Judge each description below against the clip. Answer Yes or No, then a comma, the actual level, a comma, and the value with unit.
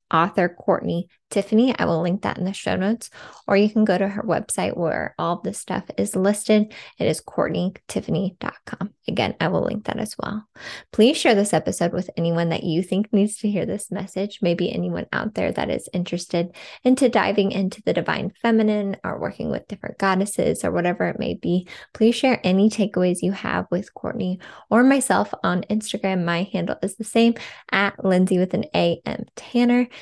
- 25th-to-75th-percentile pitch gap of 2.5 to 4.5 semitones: Yes, average, 3.3 semitones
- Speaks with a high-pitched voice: Yes, high, 195 Hz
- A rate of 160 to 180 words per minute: No, average, 190 wpm